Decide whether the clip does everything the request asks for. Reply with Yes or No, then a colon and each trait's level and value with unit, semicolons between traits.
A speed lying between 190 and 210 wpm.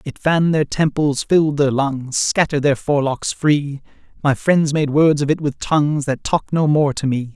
Yes: fast, 205 wpm